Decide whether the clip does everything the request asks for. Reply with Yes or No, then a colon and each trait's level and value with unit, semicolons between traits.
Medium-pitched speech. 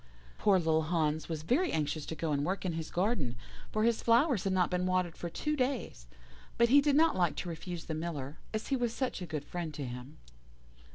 Yes: medium, 175 Hz